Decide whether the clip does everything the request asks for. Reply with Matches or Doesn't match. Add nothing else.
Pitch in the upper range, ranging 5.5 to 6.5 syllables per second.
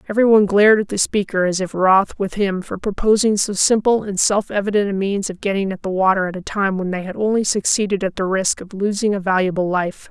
Matches